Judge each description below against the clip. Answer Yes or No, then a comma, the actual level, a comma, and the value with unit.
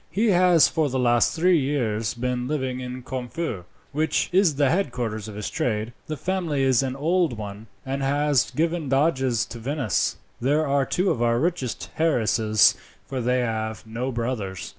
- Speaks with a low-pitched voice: Yes, low, 130 Hz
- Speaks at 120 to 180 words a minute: Yes, average, 170 wpm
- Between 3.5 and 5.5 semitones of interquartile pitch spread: Yes, average, 4.7 semitones